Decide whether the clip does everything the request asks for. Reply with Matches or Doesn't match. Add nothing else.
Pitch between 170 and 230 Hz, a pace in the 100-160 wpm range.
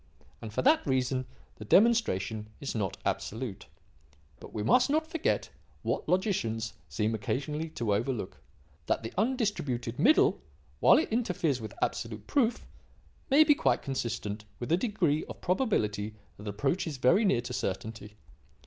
Doesn't match